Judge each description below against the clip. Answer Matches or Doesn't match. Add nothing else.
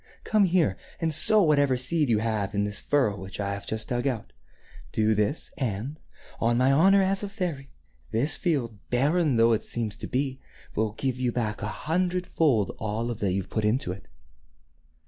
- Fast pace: Doesn't match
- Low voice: Matches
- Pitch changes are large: Matches